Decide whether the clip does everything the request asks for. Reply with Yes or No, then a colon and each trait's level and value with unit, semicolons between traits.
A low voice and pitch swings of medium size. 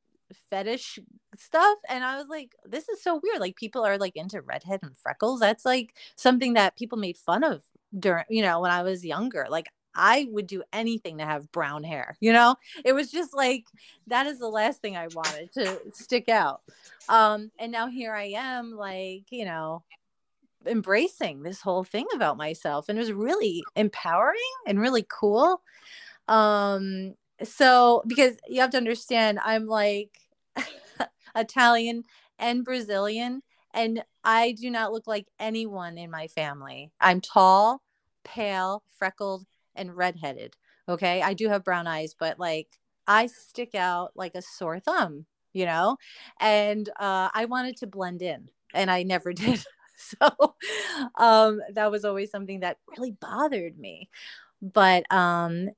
No: high, 210 Hz; average, 4.3 semitones